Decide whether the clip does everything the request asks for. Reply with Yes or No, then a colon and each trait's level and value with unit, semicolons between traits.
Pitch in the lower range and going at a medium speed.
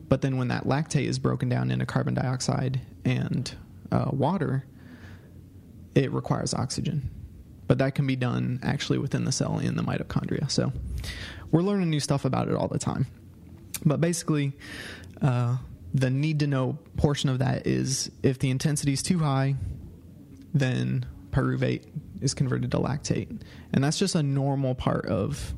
Yes: low, 130 Hz; average, 160 wpm